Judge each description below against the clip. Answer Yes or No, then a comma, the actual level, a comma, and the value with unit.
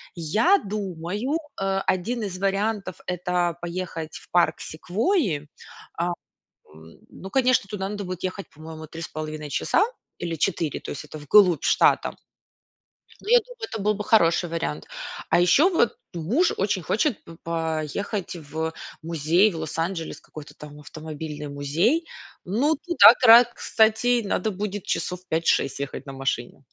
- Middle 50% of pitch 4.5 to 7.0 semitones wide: Yes, average, 5.0 semitones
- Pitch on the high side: No, medium, 180 Hz